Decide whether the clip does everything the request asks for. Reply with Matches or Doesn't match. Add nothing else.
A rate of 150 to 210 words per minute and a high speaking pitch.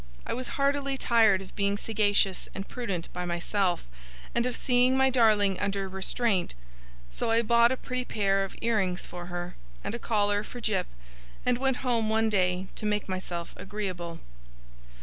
Matches